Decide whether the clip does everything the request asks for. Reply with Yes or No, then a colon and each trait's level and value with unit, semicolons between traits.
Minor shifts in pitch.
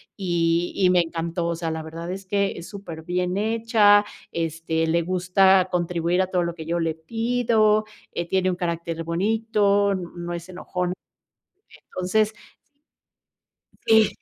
No: average, 3.0 semitones